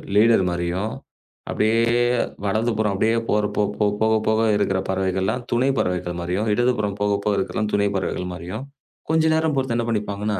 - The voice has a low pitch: Yes, low, 105 Hz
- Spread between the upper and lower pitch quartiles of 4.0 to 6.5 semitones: No, average, 2.7 semitones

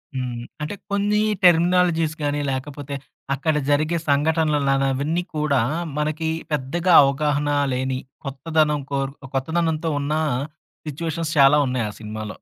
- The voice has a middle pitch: Yes, medium, 150 Hz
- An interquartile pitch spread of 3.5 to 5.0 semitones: No, average, 2.8 semitones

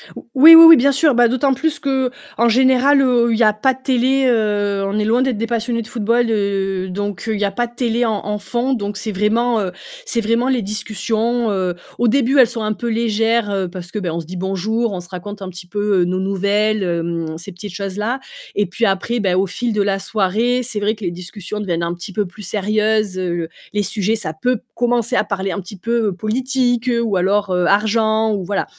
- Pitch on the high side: Yes, high, 215 Hz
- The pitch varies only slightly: No, average, 3.6 semitones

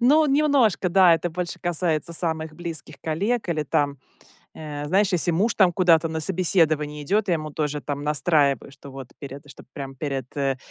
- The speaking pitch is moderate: Yes, medium, 160 Hz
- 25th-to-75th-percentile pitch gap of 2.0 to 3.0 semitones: No, average, 3.7 semitones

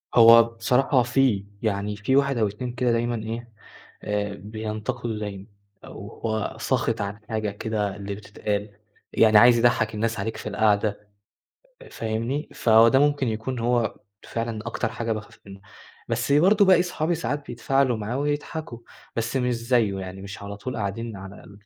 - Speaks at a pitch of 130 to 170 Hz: No, low, 115 Hz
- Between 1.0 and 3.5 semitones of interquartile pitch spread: Yes, average, 3.1 semitones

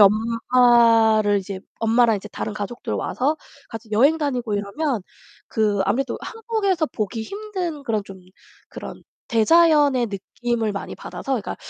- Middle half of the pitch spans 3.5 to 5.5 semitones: Yes, average, 5.2 semitones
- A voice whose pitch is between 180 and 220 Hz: No, high, 235 Hz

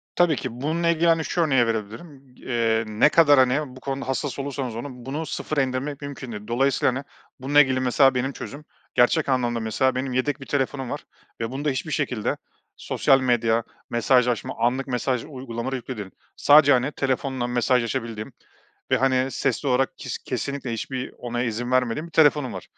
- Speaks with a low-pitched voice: Yes, low, 130 Hz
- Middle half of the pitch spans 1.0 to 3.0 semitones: Yes, narrow, 2.6 semitones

